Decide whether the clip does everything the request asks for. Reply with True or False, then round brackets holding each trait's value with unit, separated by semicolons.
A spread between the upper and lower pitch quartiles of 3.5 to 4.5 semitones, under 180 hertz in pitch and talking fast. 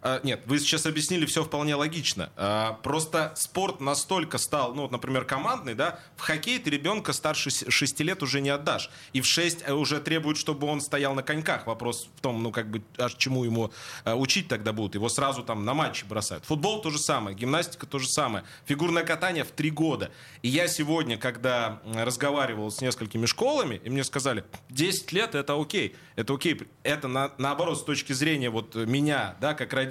True (4.1 semitones; 140 Hz; 200 wpm)